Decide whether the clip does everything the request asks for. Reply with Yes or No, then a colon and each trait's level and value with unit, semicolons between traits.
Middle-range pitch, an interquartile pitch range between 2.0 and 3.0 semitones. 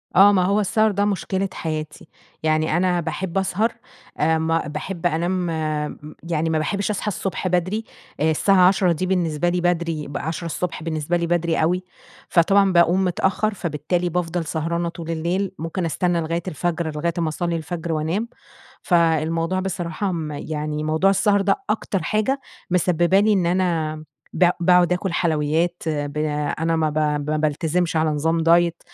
Yes: medium, 170 Hz; average, 2.7 semitones